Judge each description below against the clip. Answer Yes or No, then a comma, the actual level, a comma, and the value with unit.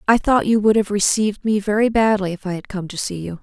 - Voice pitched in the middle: No, high, 205 Hz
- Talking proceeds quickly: Yes, fast, 280 wpm